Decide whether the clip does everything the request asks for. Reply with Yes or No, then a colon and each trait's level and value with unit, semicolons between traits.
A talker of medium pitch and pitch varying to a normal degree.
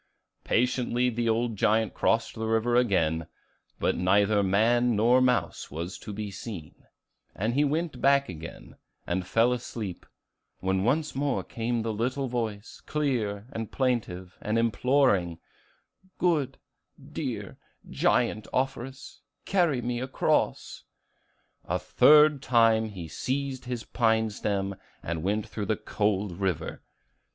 No: low, 115 Hz; average, 3.9 semitones